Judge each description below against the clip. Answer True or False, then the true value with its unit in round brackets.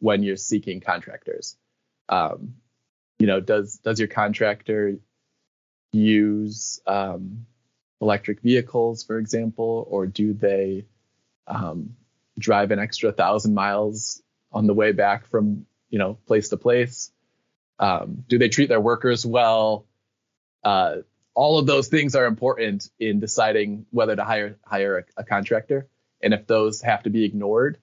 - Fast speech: False (140 wpm)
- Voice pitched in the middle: False (110 Hz)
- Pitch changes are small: True (2.2 semitones)